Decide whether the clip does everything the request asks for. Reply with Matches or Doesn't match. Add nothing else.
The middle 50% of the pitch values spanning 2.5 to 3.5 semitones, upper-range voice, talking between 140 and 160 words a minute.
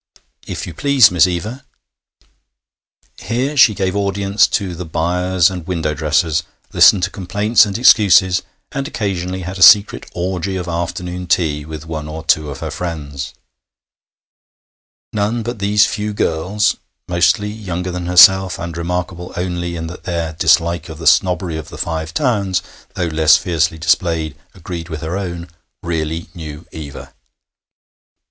Doesn't match